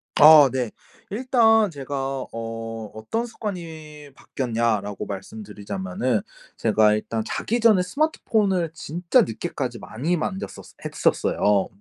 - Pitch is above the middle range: No, medium, 140 Hz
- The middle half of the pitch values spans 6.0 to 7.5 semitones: No, wide, 8.8 semitones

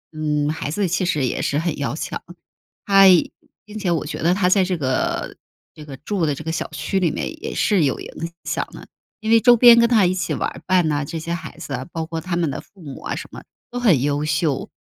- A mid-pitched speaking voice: Yes, medium, 165 Hz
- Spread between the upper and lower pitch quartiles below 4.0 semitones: No, average, 4.5 semitones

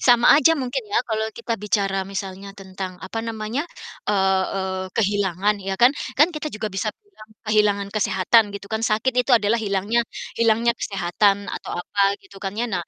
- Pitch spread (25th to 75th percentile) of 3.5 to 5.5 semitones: No, average, 2.9 semitones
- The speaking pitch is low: No, high, 210 Hz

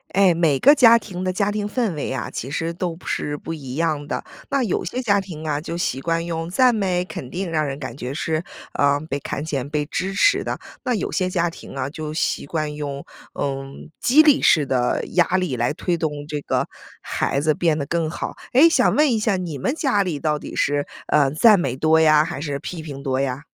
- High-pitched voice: No, medium, 160 Hz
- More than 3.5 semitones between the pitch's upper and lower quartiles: Yes, average, 4.5 semitones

